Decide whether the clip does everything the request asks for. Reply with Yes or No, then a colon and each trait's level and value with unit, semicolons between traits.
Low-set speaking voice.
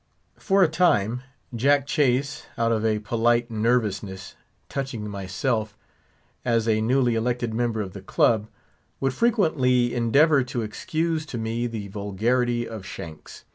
Yes: low, 120 Hz